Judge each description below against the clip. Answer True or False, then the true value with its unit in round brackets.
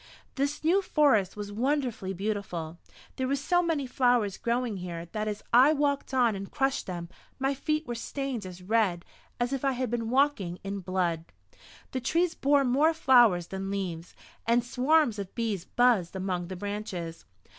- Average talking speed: True (170 wpm)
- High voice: True (230 Hz)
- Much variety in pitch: True (6.1 semitones)